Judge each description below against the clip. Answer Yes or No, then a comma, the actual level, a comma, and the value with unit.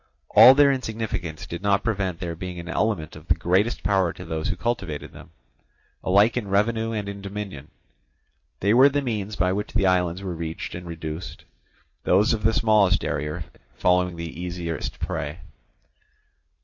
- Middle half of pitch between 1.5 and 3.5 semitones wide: No, average, 3.9 semitones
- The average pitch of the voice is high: No, very low, 95 Hz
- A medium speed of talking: Yes, average, 165 wpm